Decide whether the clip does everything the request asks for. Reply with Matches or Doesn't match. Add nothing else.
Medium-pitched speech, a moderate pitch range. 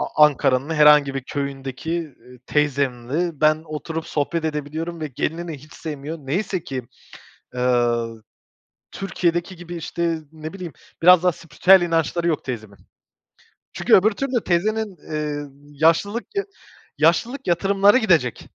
Matches